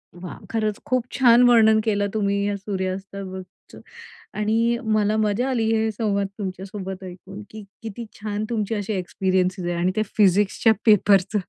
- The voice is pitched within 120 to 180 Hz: No, high, 205 Hz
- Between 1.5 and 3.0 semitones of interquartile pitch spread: Yes, narrow, 2.4 semitones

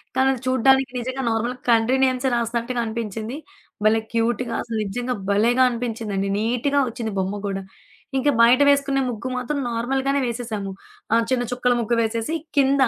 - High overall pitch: Yes, high, 240 Hz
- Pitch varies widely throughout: No, narrow, 2.5 semitones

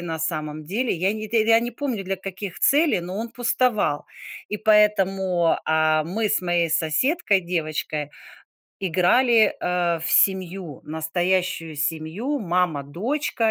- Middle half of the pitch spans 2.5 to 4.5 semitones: No, average, 5.0 semitones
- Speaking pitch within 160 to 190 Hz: Yes, medium, 185 Hz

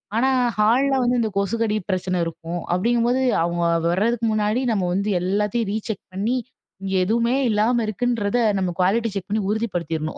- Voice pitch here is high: Yes, high, 210 Hz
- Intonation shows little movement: No, average, 3.8 semitones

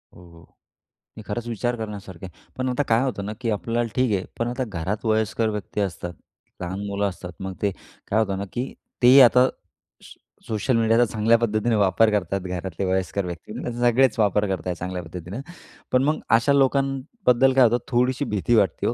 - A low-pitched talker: Yes, low, 110 Hz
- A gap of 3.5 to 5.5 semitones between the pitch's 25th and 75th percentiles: Yes, average, 4.2 semitones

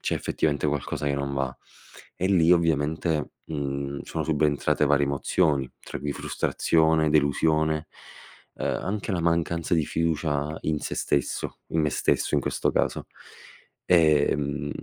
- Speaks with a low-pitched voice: Yes, very low, 75 Hz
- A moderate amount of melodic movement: No, narrow, 2.3 semitones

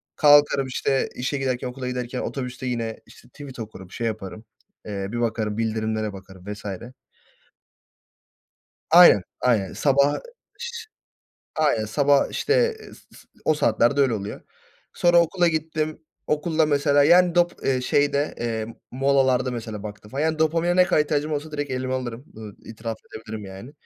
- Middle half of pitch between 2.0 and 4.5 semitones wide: No, average, 5.2 semitones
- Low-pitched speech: Yes, low, 130 Hz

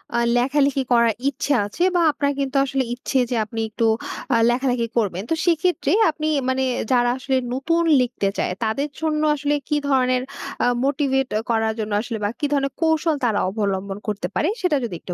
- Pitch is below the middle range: No, very high, 265 Hz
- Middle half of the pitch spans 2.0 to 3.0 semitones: No, average, 4.1 semitones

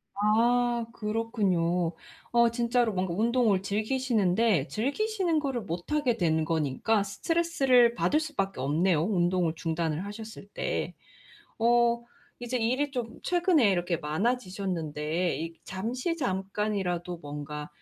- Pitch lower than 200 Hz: No, high, 210 Hz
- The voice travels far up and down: Yes, wide, 5.7 semitones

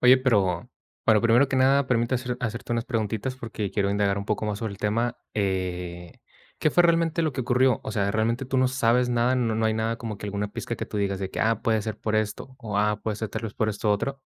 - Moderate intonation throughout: Yes, average, 3.3 semitones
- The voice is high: No, low, 110 Hz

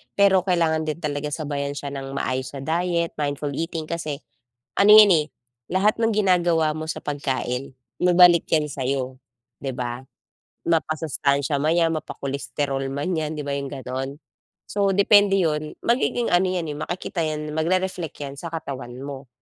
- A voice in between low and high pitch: Yes, medium, 155 Hz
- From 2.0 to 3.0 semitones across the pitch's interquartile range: No, average, 3.8 semitones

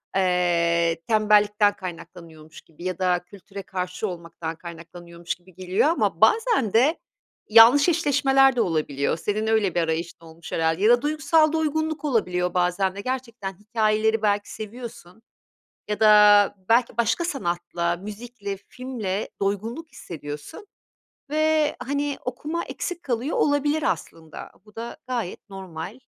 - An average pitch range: No, wide, 6.3 semitones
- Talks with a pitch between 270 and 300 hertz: No, high, 205 Hz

